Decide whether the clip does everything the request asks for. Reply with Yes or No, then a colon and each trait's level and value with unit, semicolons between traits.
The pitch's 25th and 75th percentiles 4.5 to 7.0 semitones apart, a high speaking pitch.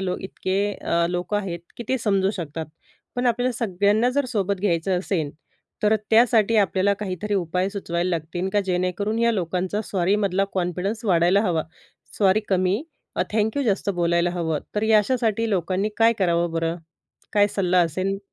No: average, 3.1 semitones; high, 195 Hz